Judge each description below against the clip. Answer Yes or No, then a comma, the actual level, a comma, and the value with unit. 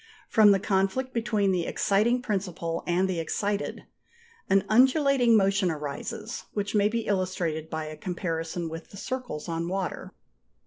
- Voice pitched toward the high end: Yes, high, 195 Hz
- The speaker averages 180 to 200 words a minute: No, average, 145 wpm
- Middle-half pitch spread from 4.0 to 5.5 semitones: Yes, average, 4.3 semitones